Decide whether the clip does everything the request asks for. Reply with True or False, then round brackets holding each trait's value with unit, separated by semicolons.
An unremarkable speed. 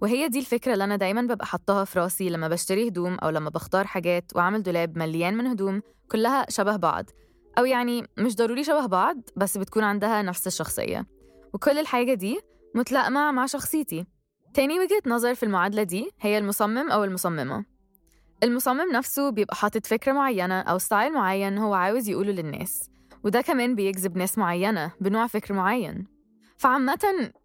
False (160 wpm)